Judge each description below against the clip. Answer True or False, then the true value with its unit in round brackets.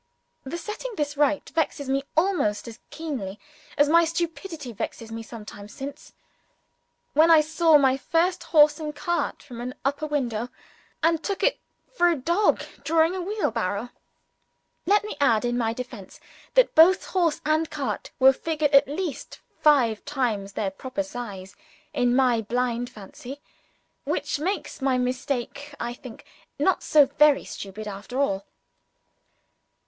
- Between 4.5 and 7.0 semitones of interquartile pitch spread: True (5.1 semitones)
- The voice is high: True (280 Hz)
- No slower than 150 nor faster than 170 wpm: True (155 wpm)